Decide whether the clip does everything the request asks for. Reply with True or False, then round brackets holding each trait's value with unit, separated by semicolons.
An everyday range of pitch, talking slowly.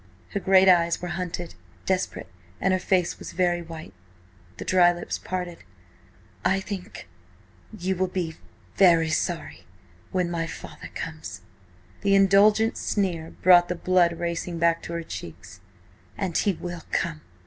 False (2.1 semitones; 130 wpm)